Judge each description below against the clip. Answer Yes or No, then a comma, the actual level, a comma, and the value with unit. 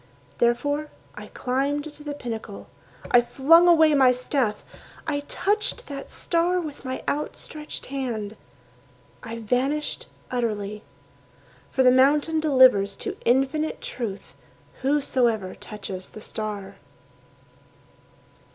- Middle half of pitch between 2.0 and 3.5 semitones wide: No, average, 4.7 semitones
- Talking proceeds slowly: Yes, slow, 105 wpm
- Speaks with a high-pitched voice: Yes, very high, 260 Hz